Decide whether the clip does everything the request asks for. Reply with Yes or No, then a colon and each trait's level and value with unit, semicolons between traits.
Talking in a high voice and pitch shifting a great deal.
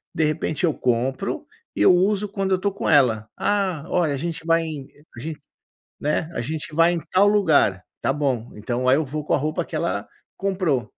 No: medium, 155 Hz; wide, 5.7 semitones